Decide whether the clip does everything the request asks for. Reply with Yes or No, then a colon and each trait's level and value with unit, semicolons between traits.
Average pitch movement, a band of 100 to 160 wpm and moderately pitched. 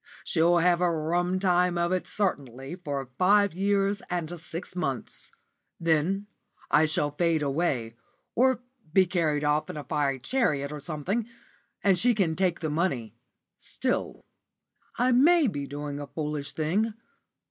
Yes: average, 4.3 semitones; average, 145 wpm; medium, 170 Hz